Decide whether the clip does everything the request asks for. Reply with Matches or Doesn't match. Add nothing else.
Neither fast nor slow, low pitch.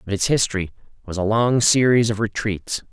Matches